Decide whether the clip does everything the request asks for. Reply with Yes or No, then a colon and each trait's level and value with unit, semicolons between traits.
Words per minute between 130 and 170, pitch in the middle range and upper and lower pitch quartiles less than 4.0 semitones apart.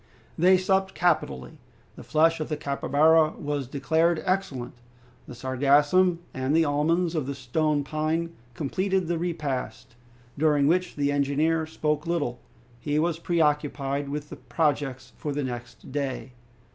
Yes: slow, 135 wpm; medium, 150 Hz; average, 2.8 semitones